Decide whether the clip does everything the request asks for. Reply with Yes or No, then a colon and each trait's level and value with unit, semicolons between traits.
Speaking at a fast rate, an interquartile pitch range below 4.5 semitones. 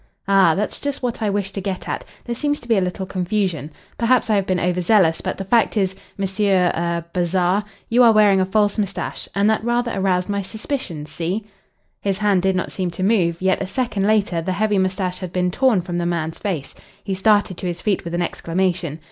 Yes: fast, 225 wpm; average, 2.8 semitones